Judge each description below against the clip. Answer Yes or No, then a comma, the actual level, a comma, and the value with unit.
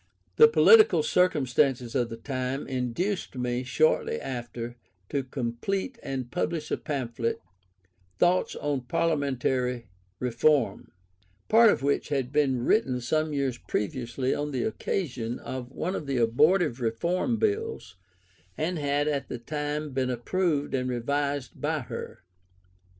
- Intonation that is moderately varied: Yes, average, 4.0 semitones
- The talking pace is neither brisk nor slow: No, slow, 130 wpm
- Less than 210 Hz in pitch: Yes, low, 135 Hz